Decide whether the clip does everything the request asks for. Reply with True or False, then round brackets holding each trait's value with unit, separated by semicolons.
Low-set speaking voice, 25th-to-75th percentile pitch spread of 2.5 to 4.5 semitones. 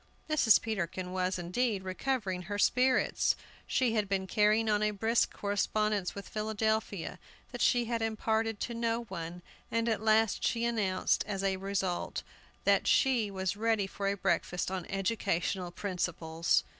False (205 Hz; 3.1 semitones)